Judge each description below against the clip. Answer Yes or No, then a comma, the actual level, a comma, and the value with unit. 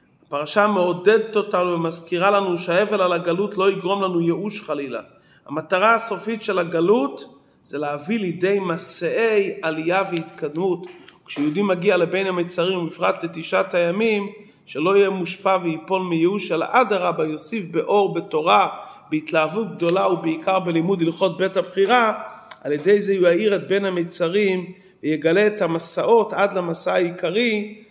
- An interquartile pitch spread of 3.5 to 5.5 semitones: No, average, 3.1 semitones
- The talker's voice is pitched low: No, medium, 185 Hz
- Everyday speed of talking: No, slow, 130 wpm